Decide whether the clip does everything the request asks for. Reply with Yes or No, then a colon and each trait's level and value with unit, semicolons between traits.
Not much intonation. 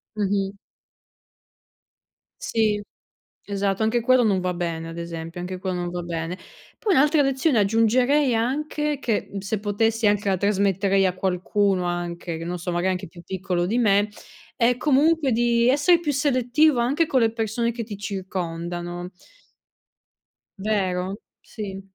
No: average, 5.0 semitones